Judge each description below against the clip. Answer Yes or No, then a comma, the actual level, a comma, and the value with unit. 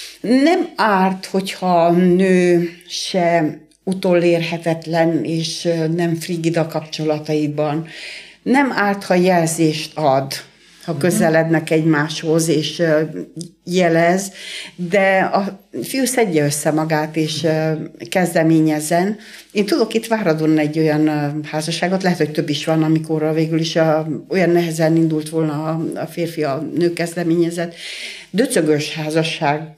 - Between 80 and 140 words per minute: Yes, average, 115 wpm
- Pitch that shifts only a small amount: Yes, narrow, 2.2 semitones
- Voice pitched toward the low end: No, medium, 165 Hz